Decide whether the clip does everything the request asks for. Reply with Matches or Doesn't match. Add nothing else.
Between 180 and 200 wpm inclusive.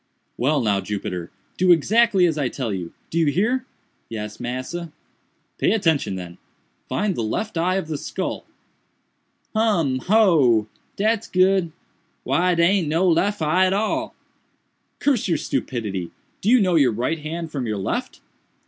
Doesn't match